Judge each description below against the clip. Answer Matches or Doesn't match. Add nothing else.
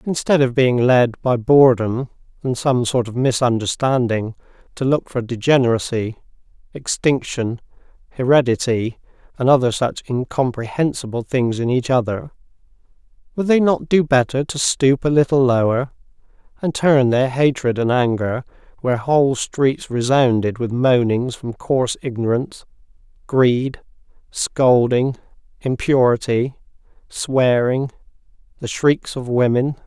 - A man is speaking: Matches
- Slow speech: Matches